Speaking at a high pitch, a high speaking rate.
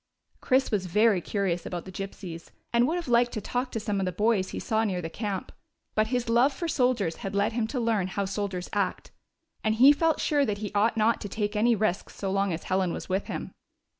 Yes: high, 210 Hz; fast, 235 wpm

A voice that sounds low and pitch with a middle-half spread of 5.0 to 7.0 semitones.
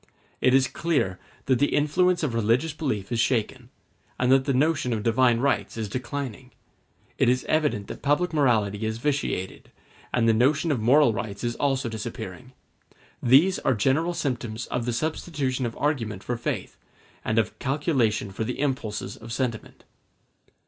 No: low, 125 Hz; average, 4.1 semitones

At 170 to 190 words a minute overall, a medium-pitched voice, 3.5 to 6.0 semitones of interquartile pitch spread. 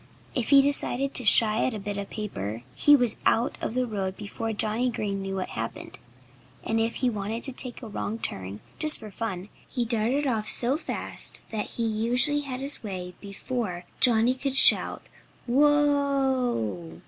No: average, 180 wpm; high, 225 Hz; average, 4.2 semitones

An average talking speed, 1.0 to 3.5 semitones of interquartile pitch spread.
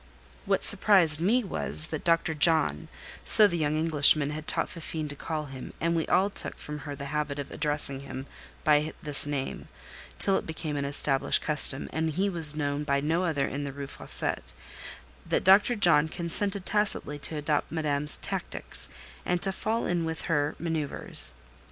Yes: average, 175 wpm; average, 2.7 semitones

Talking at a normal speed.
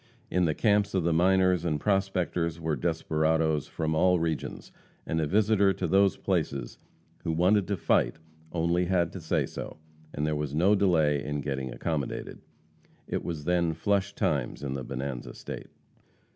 Yes: average, 165 wpm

